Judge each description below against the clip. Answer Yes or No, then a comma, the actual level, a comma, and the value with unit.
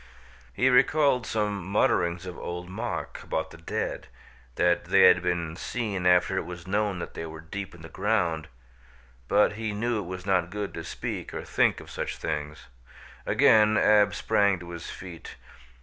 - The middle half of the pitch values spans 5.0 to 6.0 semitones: No, average, 3.4 semitones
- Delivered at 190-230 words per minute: No, average, 175 wpm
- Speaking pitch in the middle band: No, very low, 95 Hz